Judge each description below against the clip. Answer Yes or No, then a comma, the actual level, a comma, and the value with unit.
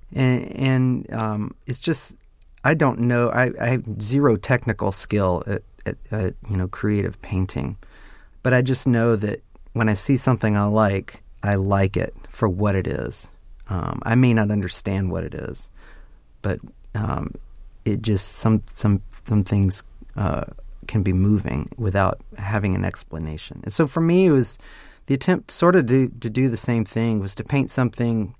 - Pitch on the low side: Yes, low, 110 Hz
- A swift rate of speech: No, average, 175 wpm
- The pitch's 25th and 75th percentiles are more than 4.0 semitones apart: Yes, average, 4.5 semitones